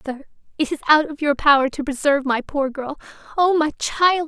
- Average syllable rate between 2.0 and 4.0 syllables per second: No, 5.4 syllables/s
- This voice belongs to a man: No, female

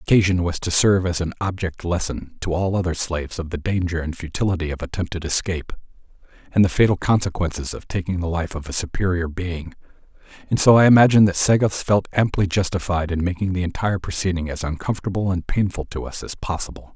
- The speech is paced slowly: No, average, 195 wpm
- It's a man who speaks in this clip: Yes, male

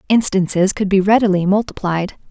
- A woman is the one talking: Yes, female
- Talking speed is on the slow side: Yes, slow, 130 wpm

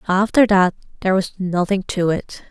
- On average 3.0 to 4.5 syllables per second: No, 5.1 syllables/s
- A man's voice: No, female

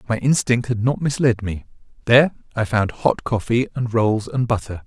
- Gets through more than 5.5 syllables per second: No, 5.1 syllables/s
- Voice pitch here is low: Yes, low, 115 Hz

